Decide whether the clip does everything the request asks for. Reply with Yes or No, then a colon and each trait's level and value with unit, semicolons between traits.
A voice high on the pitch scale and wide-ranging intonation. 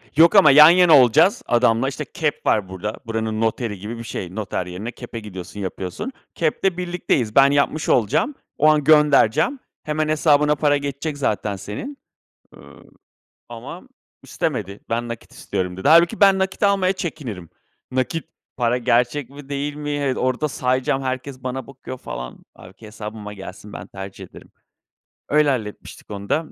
No: low, 130 Hz; wide, 5.9 semitones